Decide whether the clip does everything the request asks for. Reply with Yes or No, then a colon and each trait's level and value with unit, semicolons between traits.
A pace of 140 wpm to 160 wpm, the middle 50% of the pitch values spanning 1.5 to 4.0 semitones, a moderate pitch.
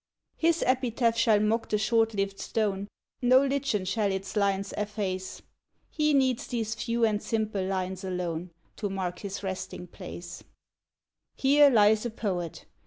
No: average, 145 wpm; average, 3.4 semitones; high, 210 Hz